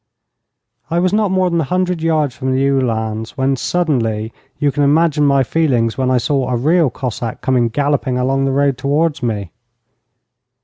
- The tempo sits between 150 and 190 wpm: Yes, average, 175 wpm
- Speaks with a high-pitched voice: No, low, 135 Hz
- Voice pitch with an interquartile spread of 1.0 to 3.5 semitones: No, average, 4.0 semitones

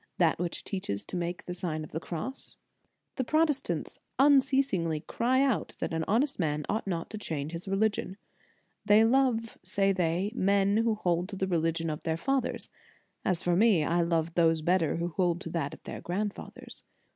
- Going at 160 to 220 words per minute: Yes, average, 190 wpm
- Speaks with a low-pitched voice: No, medium, 180 Hz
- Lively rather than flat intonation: No, average, 4.8 semitones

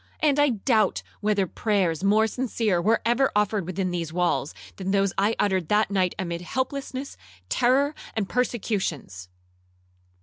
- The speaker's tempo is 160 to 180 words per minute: No, average, 140 wpm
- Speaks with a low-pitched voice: No, high, 205 Hz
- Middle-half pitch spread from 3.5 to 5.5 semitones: Yes, average, 4.5 semitones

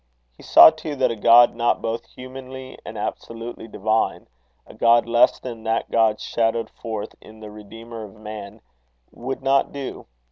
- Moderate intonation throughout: No, narrow, 1.8 semitones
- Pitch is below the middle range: Yes, low, 115 Hz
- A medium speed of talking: Yes, average, 165 wpm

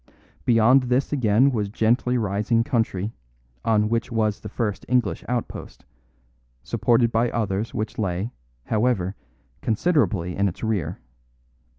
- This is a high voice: No, low, 110 Hz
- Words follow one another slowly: Yes, slow, 120 wpm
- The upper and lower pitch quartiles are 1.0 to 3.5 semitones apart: Yes, average, 2.9 semitones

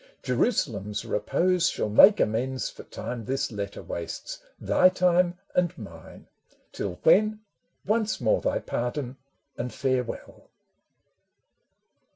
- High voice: No, low, 130 Hz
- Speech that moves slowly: Yes, slow, 110 wpm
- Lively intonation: Yes, wide, 9.0 semitones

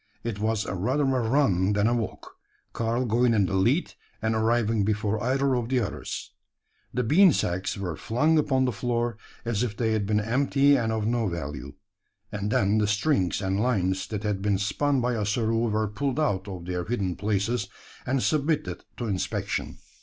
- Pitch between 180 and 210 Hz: No, low, 110 Hz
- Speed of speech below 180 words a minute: No, average, 185 wpm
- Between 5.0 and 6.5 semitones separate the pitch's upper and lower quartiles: No, average, 3.7 semitones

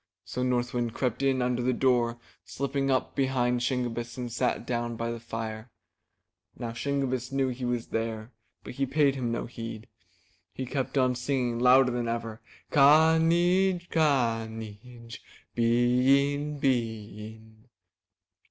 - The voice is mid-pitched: No, low, 125 Hz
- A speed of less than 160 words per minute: Yes, average, 145 wpm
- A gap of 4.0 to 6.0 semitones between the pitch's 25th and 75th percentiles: No, narrow, 2.5 semitones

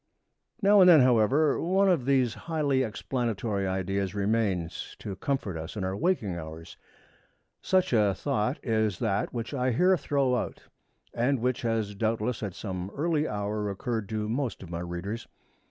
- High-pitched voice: No, low, 110 Hz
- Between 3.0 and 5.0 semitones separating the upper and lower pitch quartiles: No, wide, 5.4 semitones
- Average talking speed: Yes, average, 160 wpm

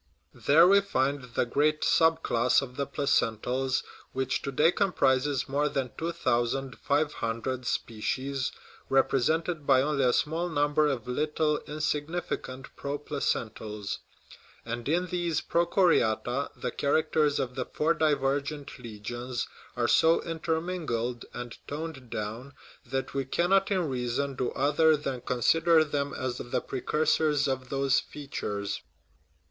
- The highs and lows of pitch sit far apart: No, average, 3.8 semitones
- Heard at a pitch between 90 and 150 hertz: Yes, medium, 140 Hz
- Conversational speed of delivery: No, slow, 130 wpm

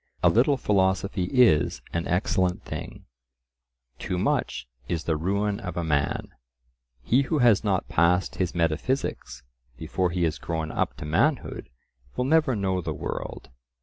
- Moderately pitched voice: No, very low, 90 Hz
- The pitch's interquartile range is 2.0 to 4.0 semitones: No, average, 4.4 semitones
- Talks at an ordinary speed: Yes, average, 150 wpm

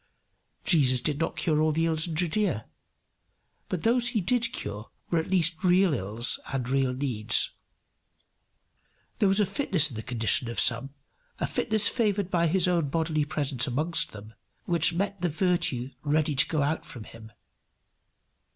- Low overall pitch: No, medium, 155 Hz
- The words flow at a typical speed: Yes, average, 165 wpm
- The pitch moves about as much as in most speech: No, wide, 5.7 semitones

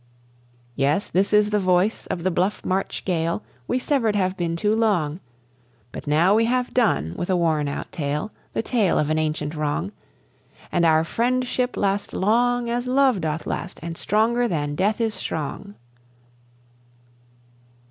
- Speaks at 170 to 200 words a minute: No, average, 160 wpm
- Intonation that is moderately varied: No, wide, 5.7 semitones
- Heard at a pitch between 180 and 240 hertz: Yes, high, 190 Hz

